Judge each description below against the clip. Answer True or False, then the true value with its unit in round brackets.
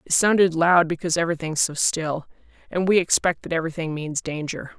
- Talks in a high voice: False (165 Hz)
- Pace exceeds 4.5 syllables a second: True (6.0 syllables/s)